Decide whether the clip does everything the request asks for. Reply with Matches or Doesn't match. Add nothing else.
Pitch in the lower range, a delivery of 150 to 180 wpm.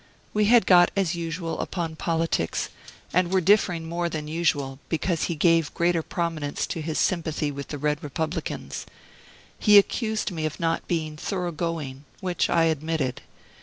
Doesn't match